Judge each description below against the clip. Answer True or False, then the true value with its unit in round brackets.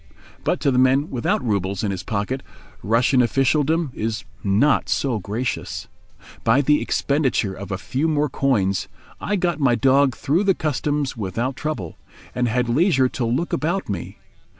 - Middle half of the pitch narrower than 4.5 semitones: False (4.9 semitones)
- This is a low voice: True (130 Hz)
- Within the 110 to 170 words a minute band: True (160 wpm)